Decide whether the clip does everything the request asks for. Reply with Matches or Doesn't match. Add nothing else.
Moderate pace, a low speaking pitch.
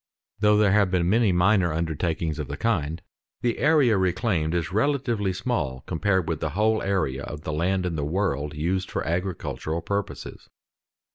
Matches